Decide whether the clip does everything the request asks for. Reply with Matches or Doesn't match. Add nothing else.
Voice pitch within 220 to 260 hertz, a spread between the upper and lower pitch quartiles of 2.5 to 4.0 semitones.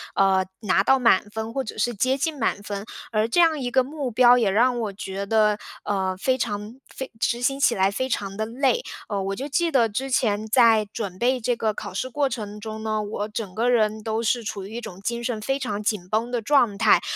Matches